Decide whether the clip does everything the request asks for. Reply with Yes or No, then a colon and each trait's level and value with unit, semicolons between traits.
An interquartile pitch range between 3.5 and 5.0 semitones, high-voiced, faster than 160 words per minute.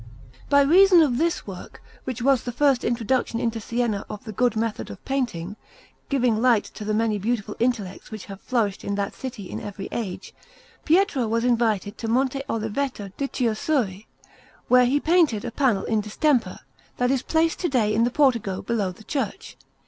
Yes: average, 4.0 semitones; high, 235 Hz; average, 180 wpm